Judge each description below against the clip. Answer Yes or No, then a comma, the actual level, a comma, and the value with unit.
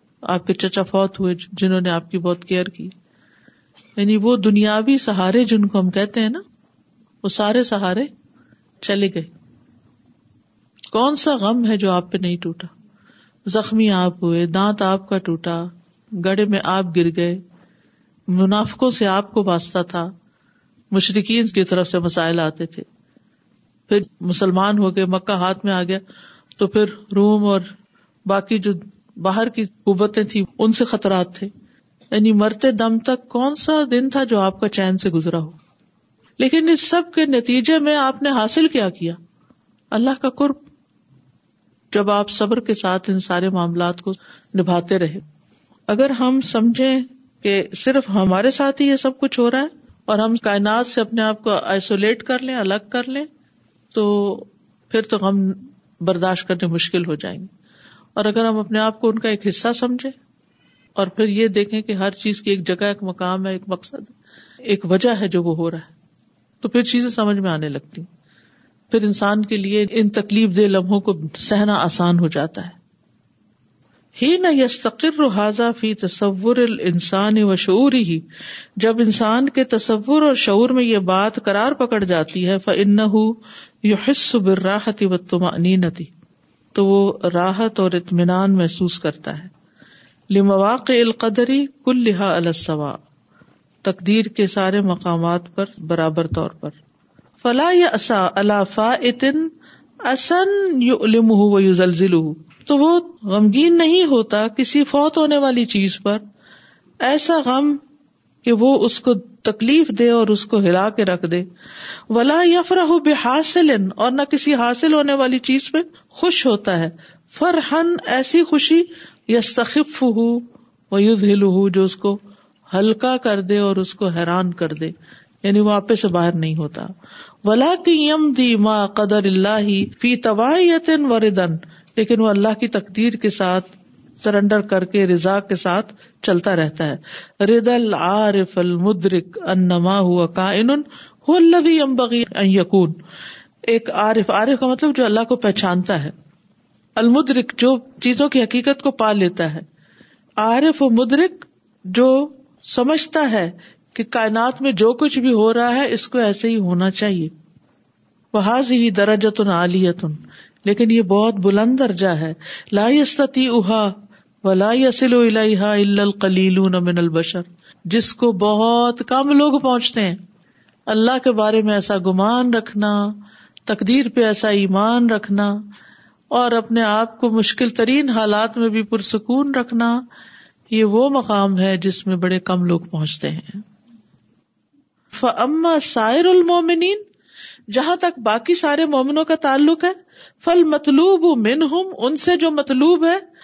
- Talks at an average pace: Yes, average, 150 wpm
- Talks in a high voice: Yes, high, 215 Hz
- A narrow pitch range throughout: No, average, 4.7 semitones